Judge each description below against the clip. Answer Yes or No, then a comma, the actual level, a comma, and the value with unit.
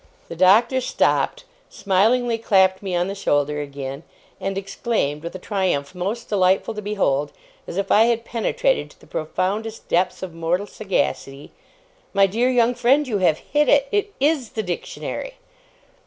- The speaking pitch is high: Yes, high, 195 Hz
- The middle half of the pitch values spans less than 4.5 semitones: No, average, 4.9 semitones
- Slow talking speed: No, average, 160 wpm